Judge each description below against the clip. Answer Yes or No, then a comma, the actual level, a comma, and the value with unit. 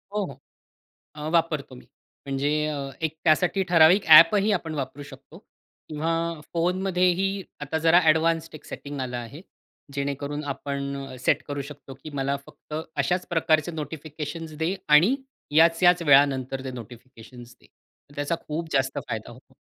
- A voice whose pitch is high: No, medium, 150 Hz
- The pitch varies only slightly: No, average, 3.3 semitones